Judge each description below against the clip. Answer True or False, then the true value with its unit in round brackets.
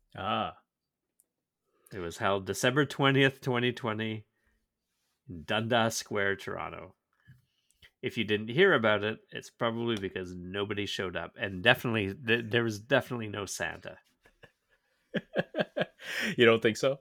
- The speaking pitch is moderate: False (110 Hz)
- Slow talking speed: True (120 wpm)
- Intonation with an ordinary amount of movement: True (3.3 semitones)